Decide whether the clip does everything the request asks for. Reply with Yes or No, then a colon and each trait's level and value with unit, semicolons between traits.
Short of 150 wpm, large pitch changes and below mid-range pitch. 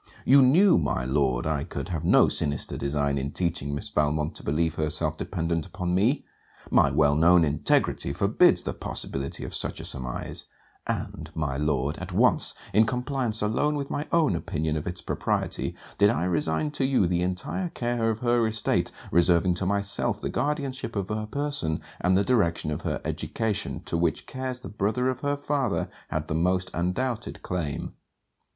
No: average, 175 wpm; wide, 7.8 semitones; very low, 90 Hz